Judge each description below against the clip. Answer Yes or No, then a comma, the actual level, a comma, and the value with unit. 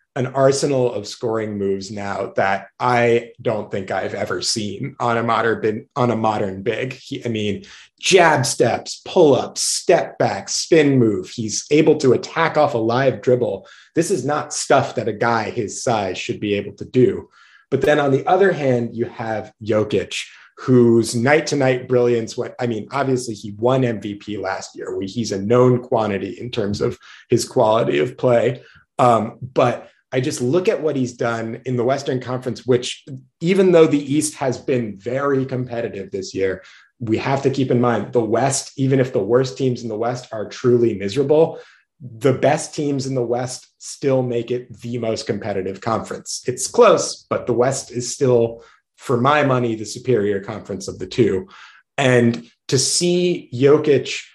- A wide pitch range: No, average, 3.1 semitones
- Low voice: Yes, low, 125 Hz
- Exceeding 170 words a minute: Yes, average, 180 wpm